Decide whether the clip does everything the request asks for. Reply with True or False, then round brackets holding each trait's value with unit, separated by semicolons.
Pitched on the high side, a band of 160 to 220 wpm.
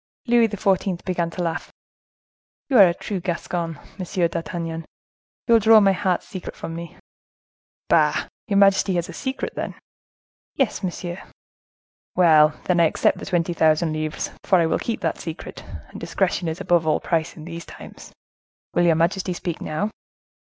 False (175 Hz; 165 wpm)